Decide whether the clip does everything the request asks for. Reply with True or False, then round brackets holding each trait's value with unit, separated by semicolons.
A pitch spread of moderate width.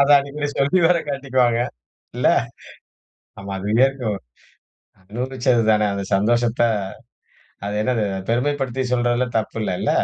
True (3.6 semitones)